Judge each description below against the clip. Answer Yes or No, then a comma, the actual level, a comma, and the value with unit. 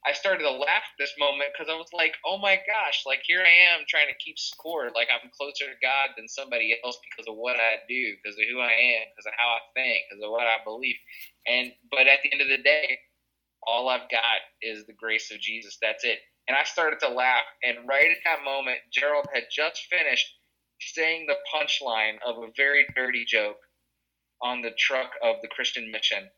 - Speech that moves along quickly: Yes, fast, 220 wpm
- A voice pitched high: No, low, 130 Hz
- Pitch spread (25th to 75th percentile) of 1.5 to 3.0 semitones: No, average, 4.0 semitones